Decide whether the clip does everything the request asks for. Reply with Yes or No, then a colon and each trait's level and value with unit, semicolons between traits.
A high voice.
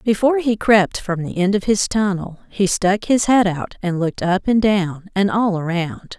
Yes: high, 195 Hz